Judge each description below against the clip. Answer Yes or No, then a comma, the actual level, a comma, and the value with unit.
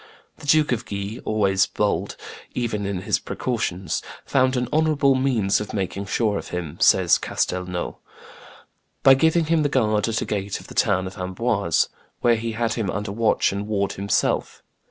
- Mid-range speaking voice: No, low, 105 Hz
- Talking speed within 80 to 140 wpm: No, average, 175 wpm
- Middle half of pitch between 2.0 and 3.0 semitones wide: No, average, 4.2 semitones